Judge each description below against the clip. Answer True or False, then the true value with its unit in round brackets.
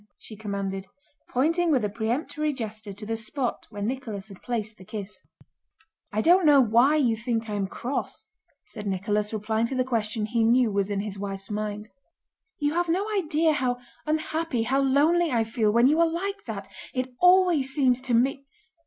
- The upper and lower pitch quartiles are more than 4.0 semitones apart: True (5.6 semitones)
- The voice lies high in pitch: True (235 Hz)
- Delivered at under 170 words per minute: False (185 wpm)